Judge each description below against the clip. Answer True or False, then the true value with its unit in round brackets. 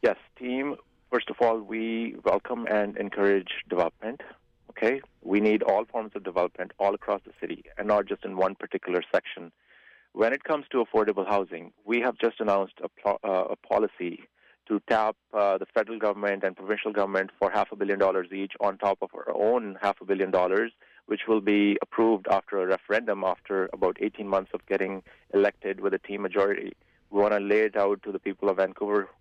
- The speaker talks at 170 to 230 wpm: True (195 wpm)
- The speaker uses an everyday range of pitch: False (1.8 semitones)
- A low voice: True (100 Hz)